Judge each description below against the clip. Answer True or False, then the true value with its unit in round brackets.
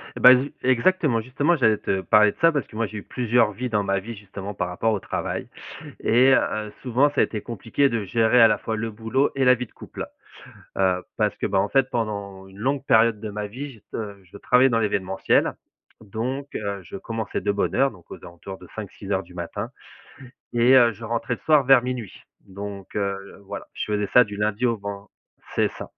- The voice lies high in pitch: False (110 Hz)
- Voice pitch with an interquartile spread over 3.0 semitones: True (3.6 semitones)